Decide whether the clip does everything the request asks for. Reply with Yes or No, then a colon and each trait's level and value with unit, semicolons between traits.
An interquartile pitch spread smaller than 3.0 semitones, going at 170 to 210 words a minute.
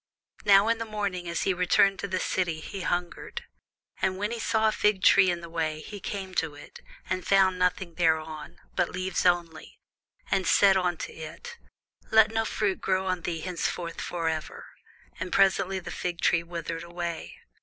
Yes: narrow, 2.6 semitones; average, 180 wpm